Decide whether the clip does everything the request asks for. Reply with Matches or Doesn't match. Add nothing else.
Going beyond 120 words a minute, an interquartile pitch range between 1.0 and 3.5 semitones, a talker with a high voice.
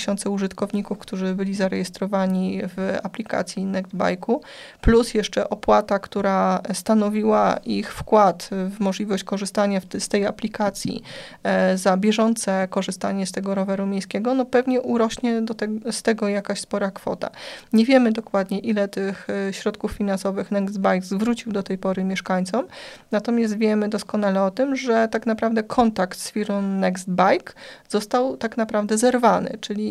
Matches